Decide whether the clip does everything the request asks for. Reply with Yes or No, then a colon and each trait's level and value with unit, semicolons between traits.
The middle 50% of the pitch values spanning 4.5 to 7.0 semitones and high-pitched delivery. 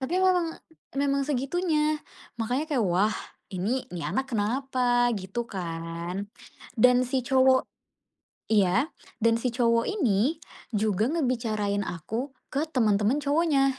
Yes: average, 5.1 semitones; high, 245 Hz